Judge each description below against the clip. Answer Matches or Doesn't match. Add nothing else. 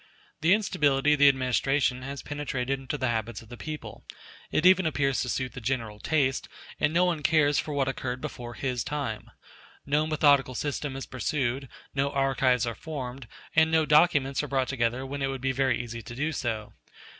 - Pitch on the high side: Doesn't match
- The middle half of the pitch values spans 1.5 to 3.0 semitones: Matches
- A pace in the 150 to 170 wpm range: Doesn't match